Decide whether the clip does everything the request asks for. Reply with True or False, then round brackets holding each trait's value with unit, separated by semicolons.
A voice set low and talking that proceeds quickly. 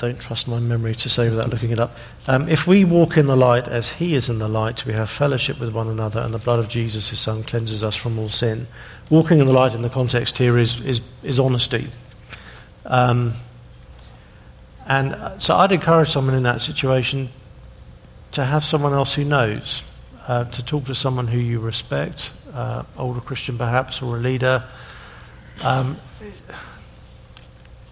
False (120 Hz; 180 wpm)